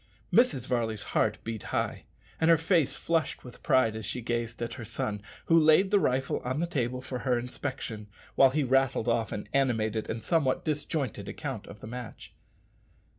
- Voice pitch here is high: No, low, 125 Hz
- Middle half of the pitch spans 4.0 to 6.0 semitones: Yes, average, 4.5 semitones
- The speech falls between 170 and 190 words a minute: Yes, average, 180 wpm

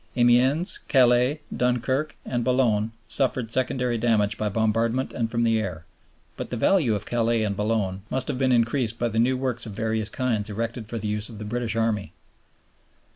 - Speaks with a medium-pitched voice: No, low, 115 Hz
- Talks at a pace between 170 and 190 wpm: Yes, average, 180 wpm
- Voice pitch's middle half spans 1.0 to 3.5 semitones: Yes, narrow, 2.5 semitones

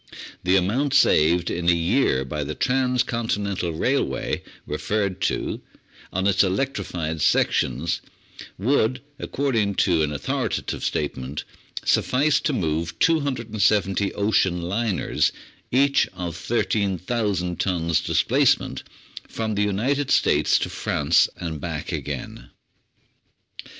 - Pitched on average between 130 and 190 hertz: No, very low, 95 Hz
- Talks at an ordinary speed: No, slow, 105 wpm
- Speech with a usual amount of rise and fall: No, wide, 5.7 semitones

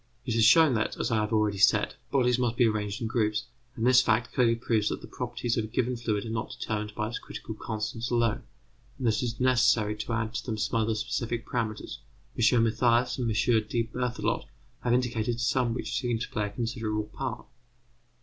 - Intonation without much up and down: Yes, narrow, 2.0 semitones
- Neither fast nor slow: No, fast, 210 wpm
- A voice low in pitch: Yes, low, 115 Hz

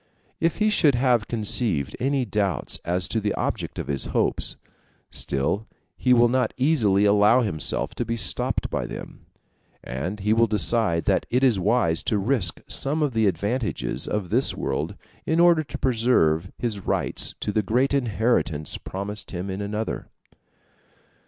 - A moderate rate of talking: Yes, average, 160 wpm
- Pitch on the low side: Yes, low, 110 Hz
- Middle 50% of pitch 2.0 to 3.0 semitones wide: No, average, 4.6 semitones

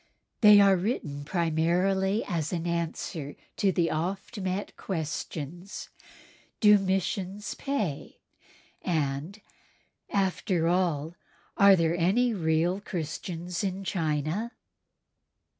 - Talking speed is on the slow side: Yes, slow, 95 wpm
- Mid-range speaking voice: Yes, medium, 180 Hz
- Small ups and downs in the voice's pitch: No, average, 3.3 semitones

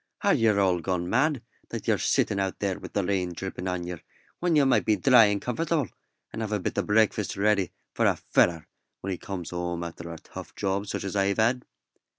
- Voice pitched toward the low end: Yes, low, 100 Hz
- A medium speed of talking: No, fast, 220 wpm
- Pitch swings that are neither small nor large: Yes, average, 3.6 semitones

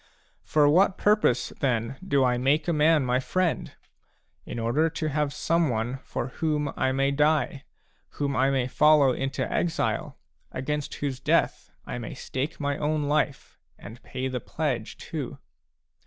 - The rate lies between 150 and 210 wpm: Yes, average, 155 wpm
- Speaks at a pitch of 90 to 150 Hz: Yes, medium, 140 Hz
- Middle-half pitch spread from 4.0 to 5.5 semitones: No, average, 2.9 semitones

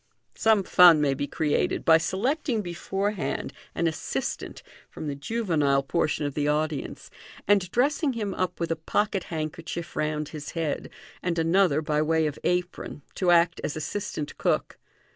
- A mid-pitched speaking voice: Yes, medium, 165 Hz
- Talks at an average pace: Yes, average, 155 wpm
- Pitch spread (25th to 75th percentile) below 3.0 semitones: No, average, 4.2 semitones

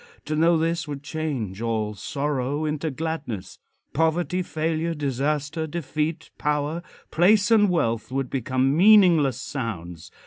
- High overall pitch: No, medium, 150 Hz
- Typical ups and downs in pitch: Yes, average, 3.8 semitones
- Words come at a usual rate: No, slow, 125 wpm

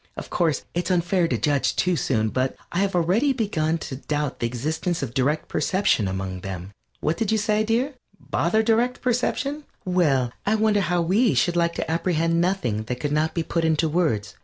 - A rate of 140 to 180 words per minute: No, average, 200 wpm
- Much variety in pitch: Yes, wide, 5.9 semitones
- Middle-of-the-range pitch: Yes, medium, 170 Hz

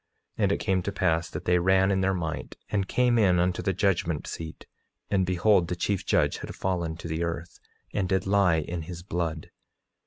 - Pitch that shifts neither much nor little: No, narrow, 2.3 semitones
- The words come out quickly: Yes, fast, 210 wpm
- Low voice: Yes, very low, 90 Hz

